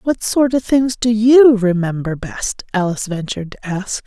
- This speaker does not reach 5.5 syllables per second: Yes, 4.6 syllables/s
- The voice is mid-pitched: No, high, 215 Hz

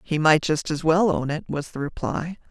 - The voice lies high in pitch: No, medium, 160 Hz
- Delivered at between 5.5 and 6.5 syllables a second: No, 4.9 syllables/s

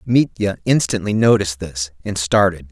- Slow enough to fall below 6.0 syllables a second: Yes, 5.0 syllables/s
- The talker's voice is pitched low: Yes, low, 100 Hz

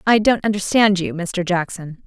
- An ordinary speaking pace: Yes, average, 175 wpm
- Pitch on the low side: No, high, 190 Hz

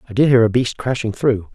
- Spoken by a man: Yes, male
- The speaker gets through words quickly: Yes, fast, 270 wpm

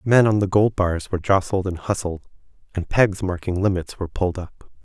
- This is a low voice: Yes, very low, 95 Hz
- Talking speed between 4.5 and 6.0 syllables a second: Yes, 5.5 syllables/s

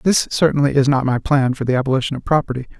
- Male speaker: Yes, male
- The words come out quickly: Yes, fast, 235 wpm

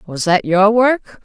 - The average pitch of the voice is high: Yes, high, 205 Hz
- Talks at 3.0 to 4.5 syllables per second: Yes, 4.4 syllables/s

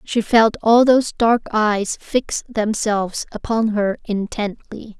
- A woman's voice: Yes, female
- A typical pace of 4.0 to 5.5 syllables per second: No, 3.8 syllables/s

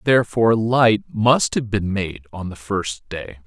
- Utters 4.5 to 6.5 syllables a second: No, 4.2 syllables/s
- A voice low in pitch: Yes, low, 105 Hz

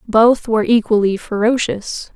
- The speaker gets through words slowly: Yes, slow, 110 wpm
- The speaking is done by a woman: Yes, female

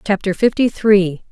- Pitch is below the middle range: No, high, 200 Hz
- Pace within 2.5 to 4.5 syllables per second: Yes, 4.2 syllables/s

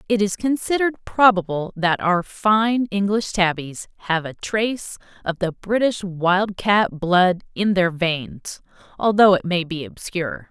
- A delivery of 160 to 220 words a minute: No, average, 150 wpm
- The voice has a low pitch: No, high, 190 Hz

